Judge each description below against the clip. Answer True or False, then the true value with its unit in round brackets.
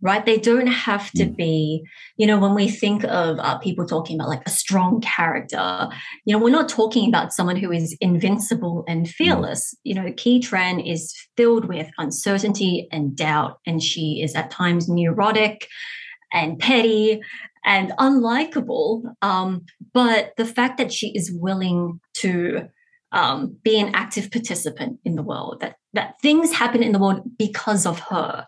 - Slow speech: False (165 wpm)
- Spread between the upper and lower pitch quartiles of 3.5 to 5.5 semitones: True (4.8 semitones)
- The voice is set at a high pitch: True (205 Hz)